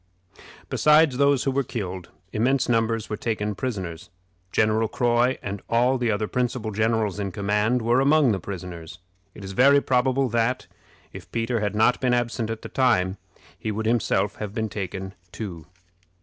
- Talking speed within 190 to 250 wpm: No, average, 165 wpm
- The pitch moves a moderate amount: Yes, average, 3.4 semitones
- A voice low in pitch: Yes, low, 110 Hz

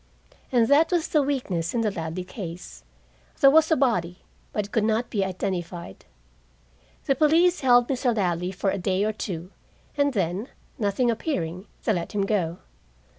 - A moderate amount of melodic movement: No, wide, 6.2 semitones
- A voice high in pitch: Yes, high, 210 Hz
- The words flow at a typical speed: Yes, average, 170 wpm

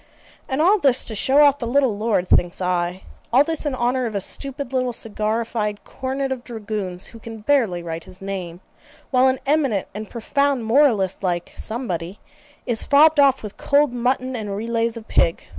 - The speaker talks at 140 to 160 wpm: No, average, 180 wpm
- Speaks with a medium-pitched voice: No, high, 235 Hz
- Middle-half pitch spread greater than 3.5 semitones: Yes, average, 4.8 semitones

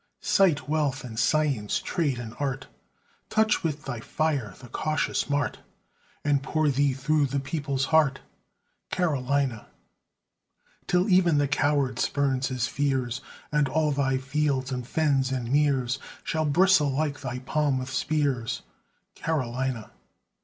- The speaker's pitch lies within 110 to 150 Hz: Yes, medium, 140 Hz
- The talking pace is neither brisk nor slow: No, slow, 130 wpm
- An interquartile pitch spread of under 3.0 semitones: Yes, narrow, 2.6 semitones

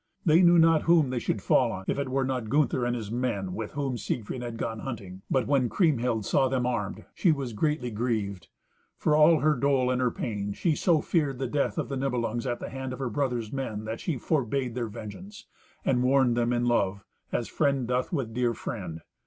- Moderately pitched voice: No, low, 125 Hz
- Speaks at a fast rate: Yes, fast, 220 wpm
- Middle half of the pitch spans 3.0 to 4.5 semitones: Yes, average, 3.4 semitones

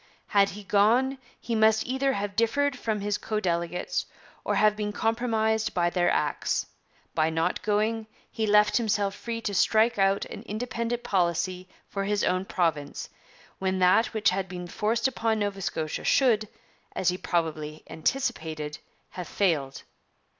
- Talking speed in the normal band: Yes, average, 155 wpm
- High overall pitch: Yes, high, 205 Hz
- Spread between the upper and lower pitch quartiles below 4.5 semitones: Yes, average, 3.8 semitones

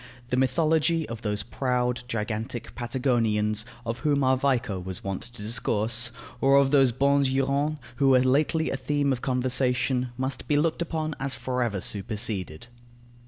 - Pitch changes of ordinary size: Yes, average, 3.3 semitones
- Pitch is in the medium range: No, low, 125 Hz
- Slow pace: No, average, 160 wpm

